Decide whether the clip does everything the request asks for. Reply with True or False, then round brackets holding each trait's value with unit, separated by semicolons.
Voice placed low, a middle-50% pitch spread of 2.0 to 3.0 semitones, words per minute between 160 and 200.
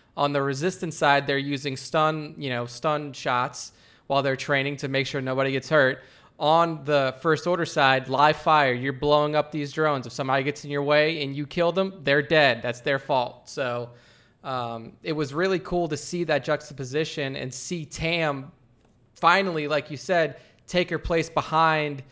False (145 Hz; 2.6 semitones; 180 wpm)